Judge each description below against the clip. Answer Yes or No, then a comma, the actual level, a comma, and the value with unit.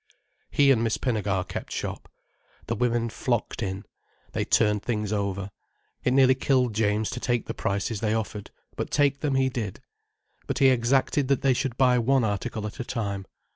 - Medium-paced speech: Yes, average, 180 wpm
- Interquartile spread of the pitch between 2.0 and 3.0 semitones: No, average, 3.9 semitones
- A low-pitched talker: Yes, low, 115 Hz